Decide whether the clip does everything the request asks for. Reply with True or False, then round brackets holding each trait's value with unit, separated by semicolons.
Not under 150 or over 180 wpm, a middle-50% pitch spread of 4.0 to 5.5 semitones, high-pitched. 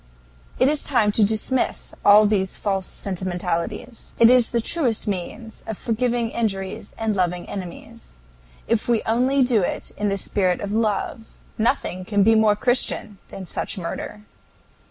False (155 wpm; 3.2 semitones; 215 Hz)